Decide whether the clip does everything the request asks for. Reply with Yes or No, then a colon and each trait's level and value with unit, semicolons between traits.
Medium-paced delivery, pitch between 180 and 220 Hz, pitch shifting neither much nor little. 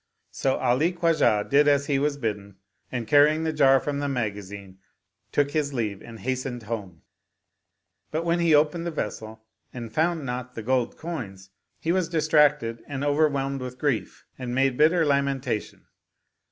No: average, 175 wpm; low, 135 Hz; average, 4.5 semitones